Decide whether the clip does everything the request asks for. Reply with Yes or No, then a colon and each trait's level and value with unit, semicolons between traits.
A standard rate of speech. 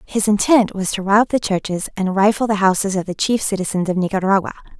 No: fast, 215 wpm